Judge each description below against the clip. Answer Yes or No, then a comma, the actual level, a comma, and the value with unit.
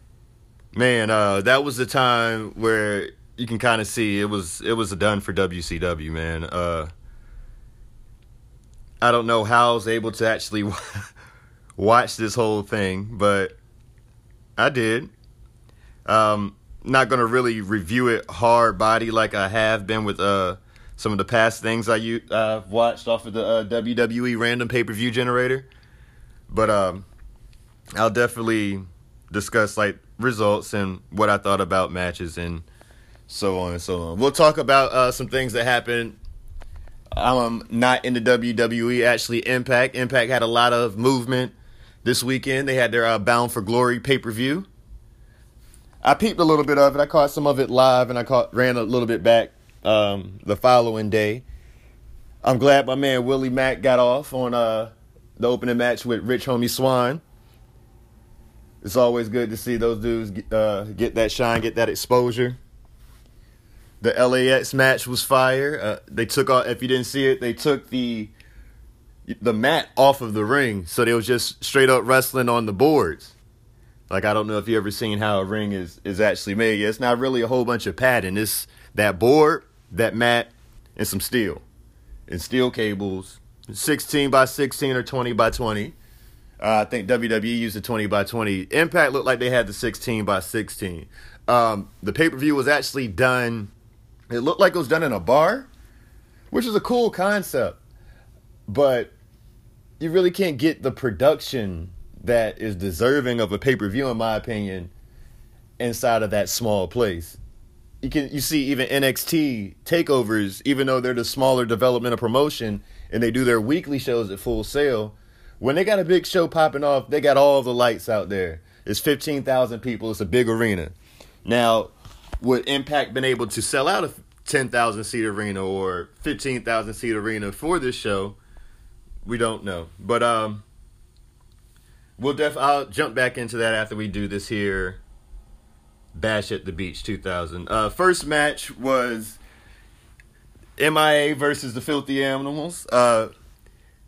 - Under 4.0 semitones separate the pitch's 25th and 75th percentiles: Yes, average, 3.0 semitones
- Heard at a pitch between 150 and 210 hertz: No, low, 115 Hz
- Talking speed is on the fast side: No, average, 170 wpm